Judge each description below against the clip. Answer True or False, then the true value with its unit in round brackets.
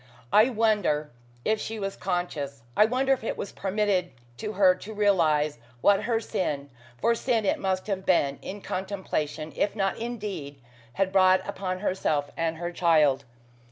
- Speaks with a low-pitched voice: False (190 Hz)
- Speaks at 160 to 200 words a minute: True (165 wpm)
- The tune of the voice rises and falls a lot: False (4.7 semitones)